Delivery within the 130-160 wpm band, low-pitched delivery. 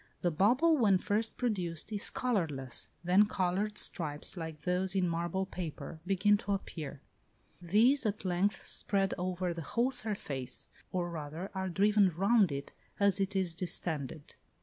No: average, 150 wpm; medium, 185 Hz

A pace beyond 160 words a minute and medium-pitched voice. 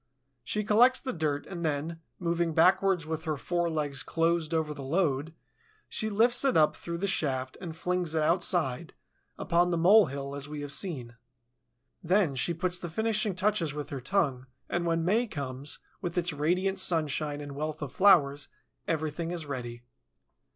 Yes: average, 170 wpm; medium, 165 Hz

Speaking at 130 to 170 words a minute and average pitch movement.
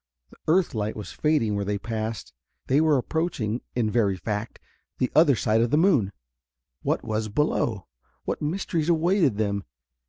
No: average, 160 wpm; wide, 6.5 semitones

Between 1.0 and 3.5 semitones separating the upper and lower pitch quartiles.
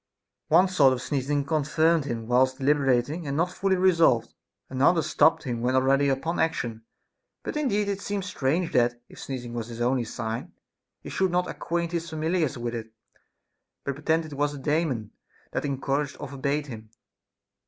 No: average, 4.7 semitones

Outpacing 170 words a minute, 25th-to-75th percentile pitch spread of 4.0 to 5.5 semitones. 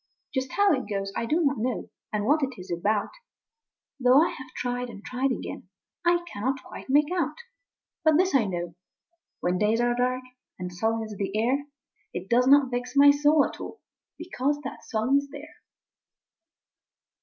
Yes: average, 180 wpm; average, 4.7 semitones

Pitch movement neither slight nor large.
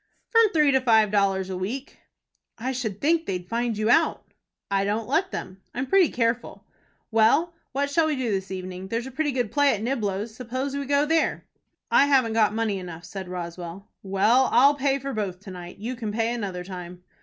No: wide, 5.9 semitones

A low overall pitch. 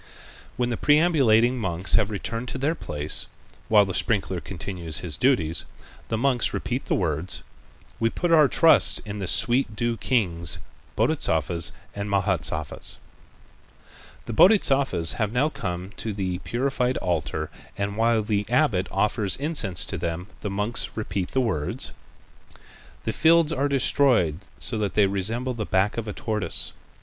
Yes: low, 105 Hz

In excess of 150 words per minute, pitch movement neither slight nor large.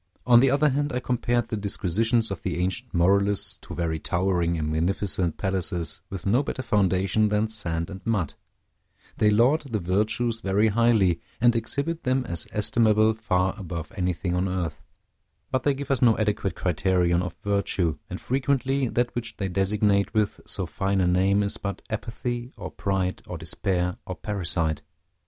Yes: average, 170 wpm; average, 4.4 semitones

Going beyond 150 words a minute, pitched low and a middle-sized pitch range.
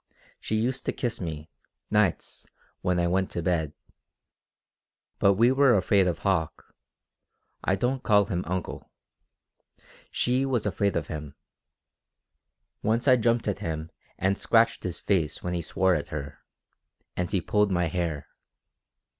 No: average, 145 wpm; very low, 95 Hz; average, 4.4 semitones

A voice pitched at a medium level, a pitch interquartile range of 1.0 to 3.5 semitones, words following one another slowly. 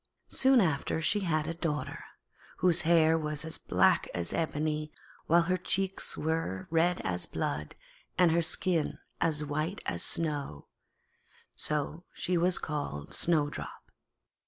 Yes: medium, 160 Hz; narrow, 2.4 semitones; slow, 130 wpm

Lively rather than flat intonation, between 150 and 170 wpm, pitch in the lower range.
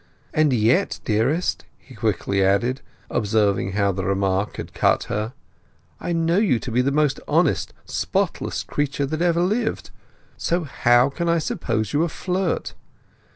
Yes: wide, 7.7 semitones; average, 155 wpm; low, 130 Hz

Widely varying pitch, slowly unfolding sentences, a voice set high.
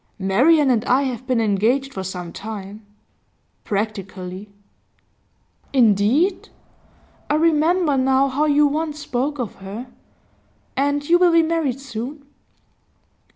Yes: wide, 5.8 semitones; slow, 115 wpm; very high, 260 Hz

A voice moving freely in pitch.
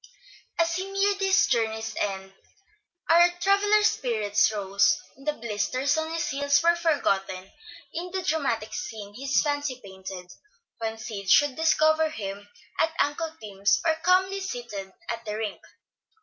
Yes: wide, 8.0 semitones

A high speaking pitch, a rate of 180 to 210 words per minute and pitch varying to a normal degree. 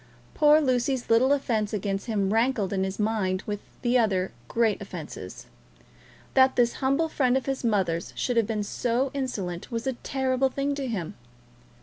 No: high, 230 Hz; average, 165 wpm; average, 4.6 semitones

